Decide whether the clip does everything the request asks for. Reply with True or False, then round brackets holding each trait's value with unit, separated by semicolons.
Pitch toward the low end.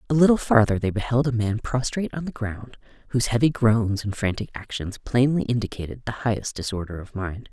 True (115 Hz)